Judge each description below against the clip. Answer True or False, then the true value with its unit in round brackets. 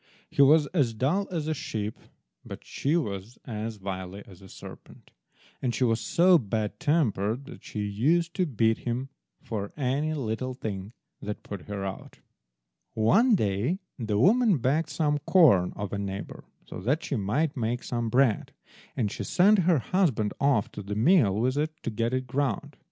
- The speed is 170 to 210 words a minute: True (175 wpm)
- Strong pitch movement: True (6.7 semitones)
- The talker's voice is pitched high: False (120 Hz)